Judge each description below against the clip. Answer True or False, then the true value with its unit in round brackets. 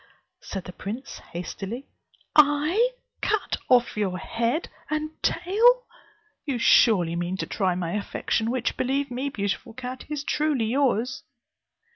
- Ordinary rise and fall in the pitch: False (6.5 semitones)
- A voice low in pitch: False (245 Hz)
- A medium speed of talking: False (130 wpm)